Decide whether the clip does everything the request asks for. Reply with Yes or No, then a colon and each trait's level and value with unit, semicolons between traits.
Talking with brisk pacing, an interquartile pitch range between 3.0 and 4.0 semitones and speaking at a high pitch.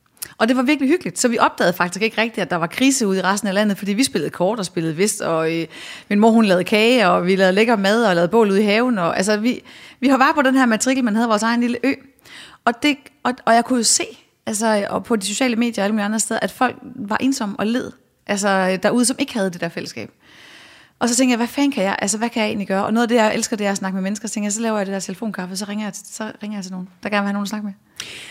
Yes: fast, 305 wpm; average, 3.4 semitones; high, 215 Hz